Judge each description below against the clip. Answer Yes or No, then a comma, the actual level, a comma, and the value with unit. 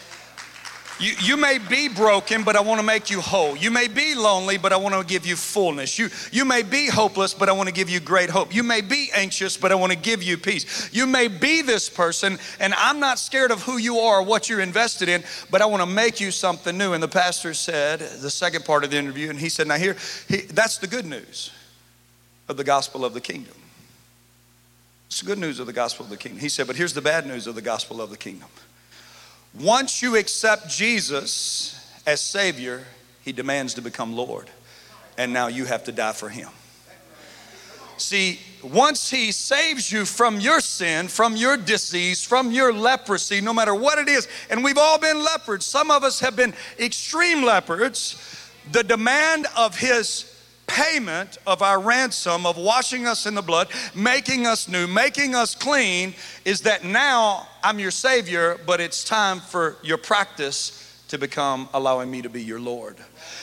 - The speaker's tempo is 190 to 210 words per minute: Yes, average, 200 wpm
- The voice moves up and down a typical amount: No, wide, 6.9 semitones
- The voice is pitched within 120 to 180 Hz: No, high, 195 Hz